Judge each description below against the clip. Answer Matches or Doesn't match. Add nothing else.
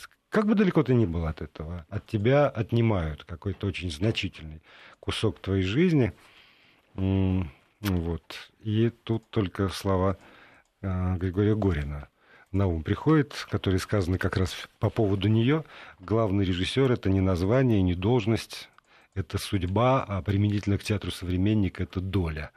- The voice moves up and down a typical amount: Matches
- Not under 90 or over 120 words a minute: Doesn't match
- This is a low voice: Matches